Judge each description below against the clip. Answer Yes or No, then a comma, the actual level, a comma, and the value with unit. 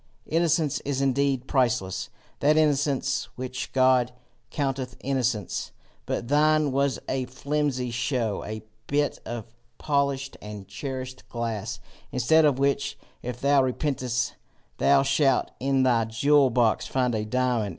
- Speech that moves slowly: Yes, slow, 130 wpm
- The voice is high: No, low, 130 Hz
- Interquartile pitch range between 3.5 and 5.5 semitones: No, narrow, 2.4 semitones